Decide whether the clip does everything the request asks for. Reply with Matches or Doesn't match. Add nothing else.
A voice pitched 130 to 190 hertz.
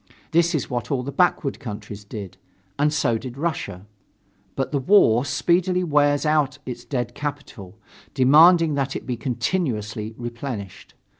Matches